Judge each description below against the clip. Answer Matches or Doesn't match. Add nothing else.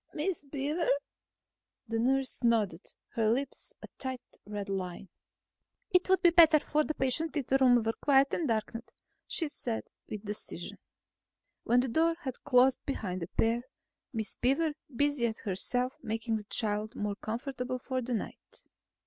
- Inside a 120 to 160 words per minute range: Matches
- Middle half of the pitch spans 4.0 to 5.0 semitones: Matches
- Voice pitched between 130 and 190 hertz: Doesn't match